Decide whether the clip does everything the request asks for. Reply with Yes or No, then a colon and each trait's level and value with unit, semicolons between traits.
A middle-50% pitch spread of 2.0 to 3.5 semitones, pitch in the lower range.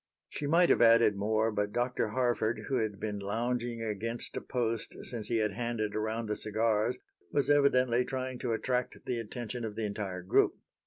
Yes: narrow, 2.5 semitones; low, 115 Hz